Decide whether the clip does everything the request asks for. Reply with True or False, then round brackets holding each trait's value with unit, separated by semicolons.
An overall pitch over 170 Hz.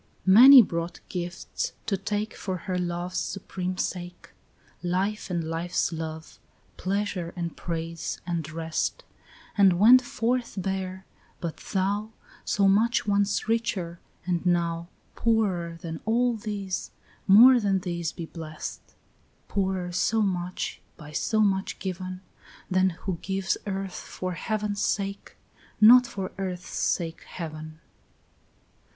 True (185 Hz)